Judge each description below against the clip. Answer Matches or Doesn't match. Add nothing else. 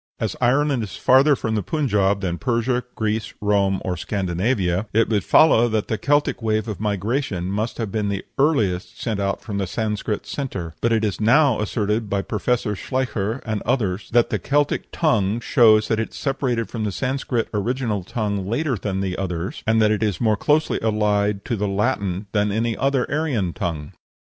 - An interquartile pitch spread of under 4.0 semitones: Matches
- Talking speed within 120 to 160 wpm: Doesn't match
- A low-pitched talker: Matches